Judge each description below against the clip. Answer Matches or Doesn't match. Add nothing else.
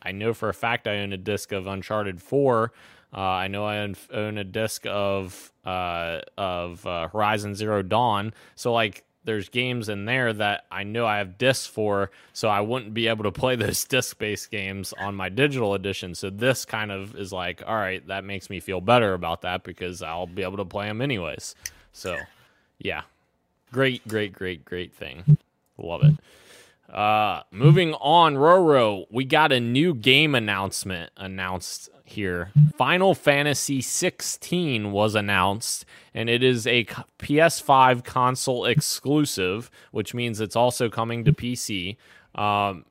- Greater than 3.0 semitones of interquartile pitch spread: Matches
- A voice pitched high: Doesn't match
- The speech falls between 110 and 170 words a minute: Matches